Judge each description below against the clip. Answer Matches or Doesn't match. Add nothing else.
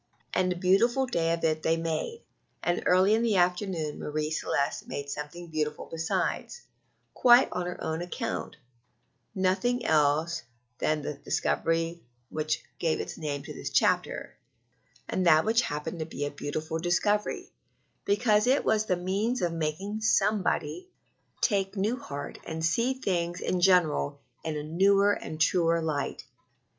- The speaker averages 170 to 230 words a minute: Doesn't match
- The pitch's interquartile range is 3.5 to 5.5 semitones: Matches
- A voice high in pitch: Doesn't match